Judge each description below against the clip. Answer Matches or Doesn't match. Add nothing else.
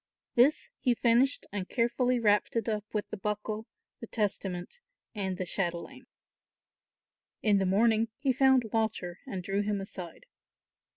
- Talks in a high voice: Matches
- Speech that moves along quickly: Doesn't match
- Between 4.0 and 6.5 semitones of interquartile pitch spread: Doesn't match